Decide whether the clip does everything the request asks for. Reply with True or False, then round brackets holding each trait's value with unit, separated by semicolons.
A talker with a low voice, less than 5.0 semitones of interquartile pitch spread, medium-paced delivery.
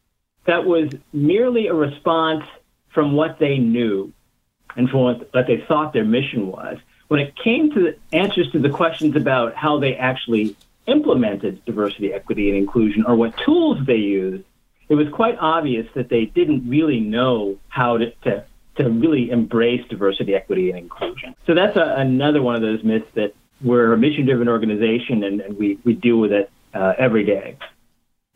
False (120 Hz; 5.5 semitones; 180 wpm)